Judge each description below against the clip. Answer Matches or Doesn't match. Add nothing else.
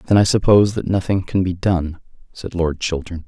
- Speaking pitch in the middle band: Doesn't match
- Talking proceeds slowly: Doesn't match